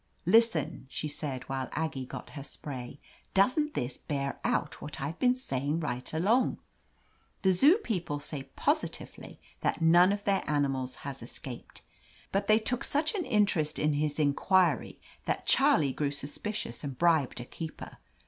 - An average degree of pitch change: No, wide, 6.2 semitones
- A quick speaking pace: No, average, 160 wpm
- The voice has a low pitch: No, medium, 150 Hz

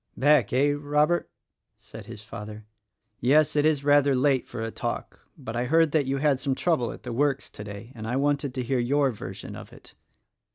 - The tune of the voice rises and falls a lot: No, average, 3.3 semitones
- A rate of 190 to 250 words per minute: Yes, average, 200 wpm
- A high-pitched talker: No, low, 135 Hz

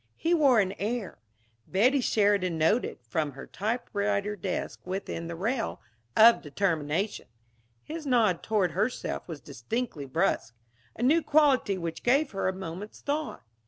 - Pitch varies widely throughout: Yes, wide, 6.4 semitones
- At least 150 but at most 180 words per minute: No, average, 140 wpm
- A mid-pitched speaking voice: No, high, 200 Hz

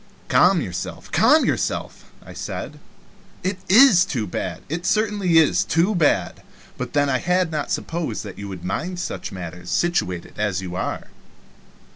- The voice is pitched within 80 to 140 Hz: No, medium, 155 Hz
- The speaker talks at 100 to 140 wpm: No, average, 160 wpm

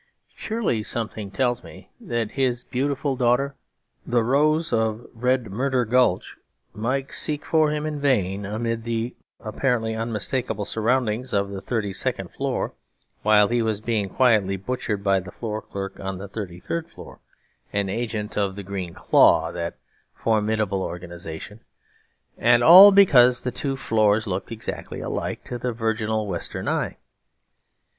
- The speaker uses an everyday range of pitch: Yes, average, 3.7 semitones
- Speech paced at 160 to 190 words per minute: No, average, 145 wpm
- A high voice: No, low, 115 Hz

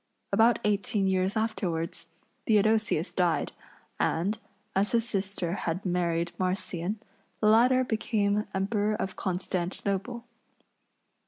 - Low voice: No, high, 200 Hz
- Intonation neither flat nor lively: Yes, average, 3.2 semitones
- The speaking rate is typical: No, slow, 100 wpm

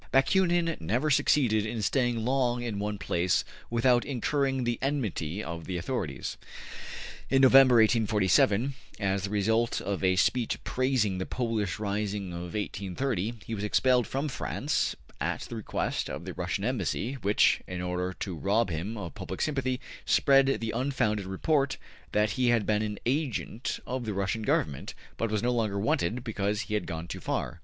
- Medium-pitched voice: No, low, 110 Hz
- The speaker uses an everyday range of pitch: Yes, average, 4.4 semitones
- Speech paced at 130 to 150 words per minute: No, average, 165 wpm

